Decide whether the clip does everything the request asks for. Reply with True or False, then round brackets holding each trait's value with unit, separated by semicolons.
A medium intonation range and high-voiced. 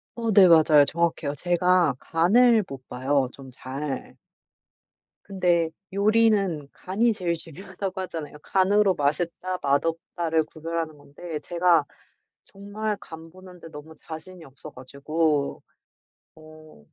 False (3.9 semitones; 165 Hz)